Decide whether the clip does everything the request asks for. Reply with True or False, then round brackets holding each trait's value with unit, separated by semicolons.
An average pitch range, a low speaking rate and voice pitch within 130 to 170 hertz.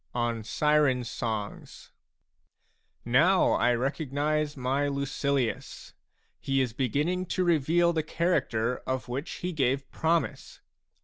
True (3.9 semitones; 110 wpm; 140 Hz)